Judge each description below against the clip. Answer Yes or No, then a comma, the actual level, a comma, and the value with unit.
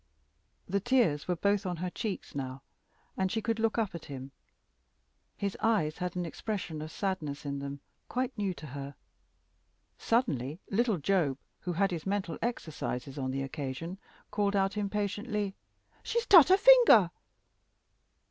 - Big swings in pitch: Yes, wide, 5.9 semitones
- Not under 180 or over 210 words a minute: No, average, 150 wpm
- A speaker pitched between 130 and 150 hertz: No, high, 190 Hz